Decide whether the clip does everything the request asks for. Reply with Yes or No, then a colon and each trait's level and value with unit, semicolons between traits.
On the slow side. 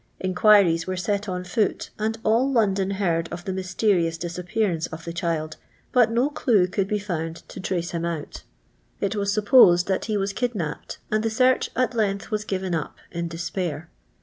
No: average, 180 wpm